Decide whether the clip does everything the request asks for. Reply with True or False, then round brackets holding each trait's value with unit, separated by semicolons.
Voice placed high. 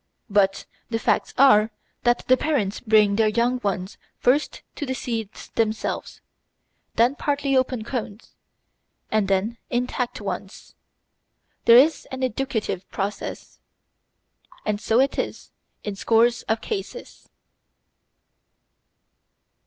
True (230 Hz)